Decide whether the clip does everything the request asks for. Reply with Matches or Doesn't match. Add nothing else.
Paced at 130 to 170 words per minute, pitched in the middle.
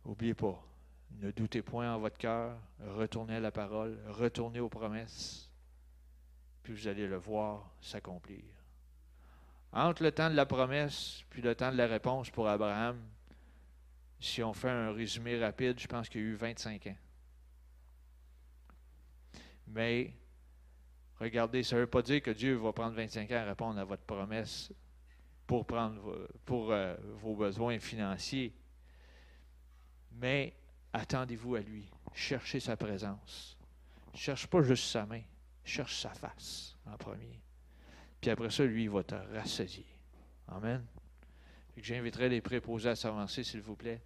Doesn't match